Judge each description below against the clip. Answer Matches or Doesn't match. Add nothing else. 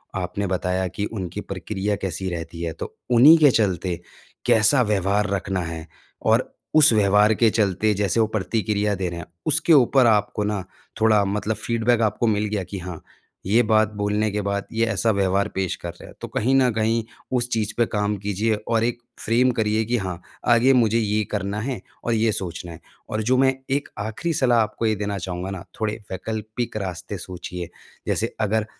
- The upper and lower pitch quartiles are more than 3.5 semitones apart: Doesn't match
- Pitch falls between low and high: Doesn't match